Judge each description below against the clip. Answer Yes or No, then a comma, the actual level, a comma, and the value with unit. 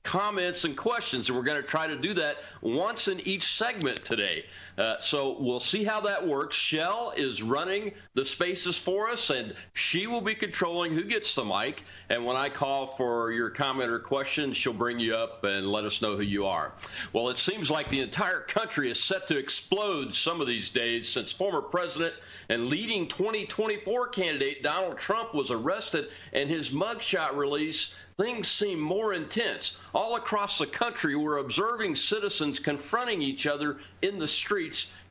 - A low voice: No, medium, 150 Hz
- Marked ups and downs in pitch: Yes, wide, 6.9 semitones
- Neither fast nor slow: Yes, average, 180 wpm